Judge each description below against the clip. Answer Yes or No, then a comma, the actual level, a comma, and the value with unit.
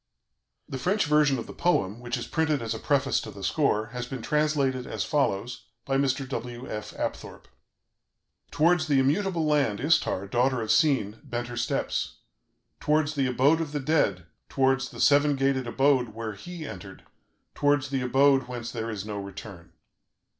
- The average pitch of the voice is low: Yes, low, 130 Hz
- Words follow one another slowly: No, average, 170 wpm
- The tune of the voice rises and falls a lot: No, average, 4.2 semitones